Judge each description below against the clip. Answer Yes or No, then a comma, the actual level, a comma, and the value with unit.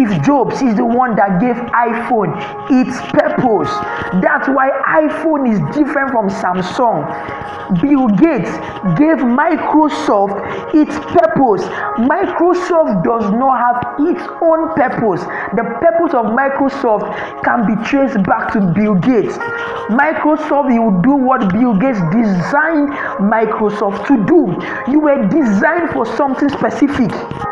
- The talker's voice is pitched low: No, very high, 265 Hz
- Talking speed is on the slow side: Yes, slow, 120 wpm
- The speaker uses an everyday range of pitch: No, wide, 5.8 semitones